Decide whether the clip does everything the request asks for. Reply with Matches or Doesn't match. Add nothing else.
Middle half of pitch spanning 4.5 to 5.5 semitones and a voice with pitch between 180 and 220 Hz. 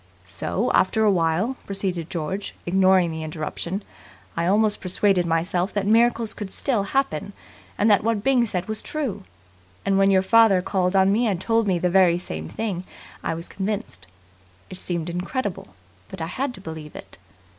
Doesn't match